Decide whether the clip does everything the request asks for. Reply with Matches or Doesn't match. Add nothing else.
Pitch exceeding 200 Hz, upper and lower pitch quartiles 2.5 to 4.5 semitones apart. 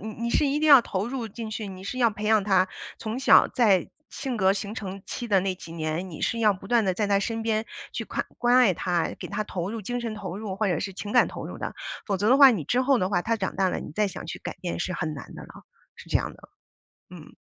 Matches